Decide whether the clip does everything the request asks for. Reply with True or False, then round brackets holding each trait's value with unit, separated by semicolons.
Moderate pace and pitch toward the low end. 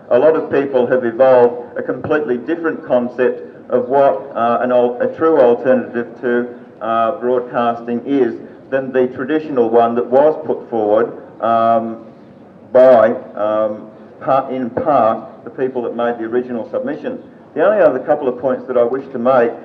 True (165 wpm; 125 Hz)